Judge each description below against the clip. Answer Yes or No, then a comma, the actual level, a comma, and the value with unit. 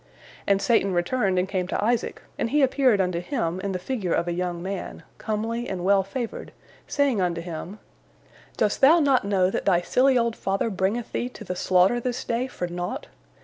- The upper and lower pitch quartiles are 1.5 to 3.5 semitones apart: No, average, 4.9 semitones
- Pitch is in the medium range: No, high, 200 Hz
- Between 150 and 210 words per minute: Yes, average, 195 wpm